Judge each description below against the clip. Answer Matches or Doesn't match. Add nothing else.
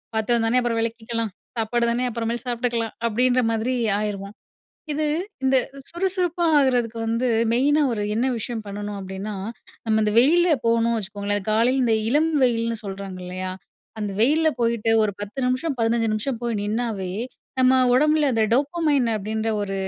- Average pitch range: Matches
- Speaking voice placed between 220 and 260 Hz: Matches